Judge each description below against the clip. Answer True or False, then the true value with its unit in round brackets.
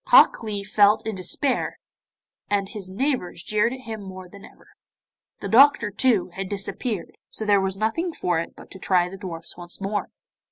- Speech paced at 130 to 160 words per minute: False (185 wpm)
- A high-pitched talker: True (200 Hz)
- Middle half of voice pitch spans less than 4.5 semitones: True (3.0 semitones)